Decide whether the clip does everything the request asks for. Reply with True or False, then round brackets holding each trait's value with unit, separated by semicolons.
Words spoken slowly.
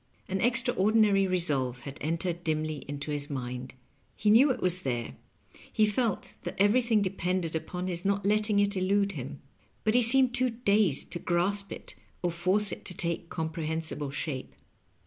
False (165 wpm)